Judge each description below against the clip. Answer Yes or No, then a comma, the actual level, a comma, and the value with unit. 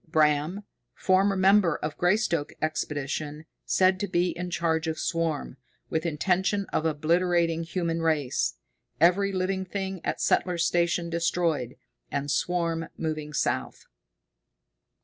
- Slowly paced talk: Yes, slow, 120 wpm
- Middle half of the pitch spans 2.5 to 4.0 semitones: Yes, average, 2.8 semitones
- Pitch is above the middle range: No, medium, 170 Hz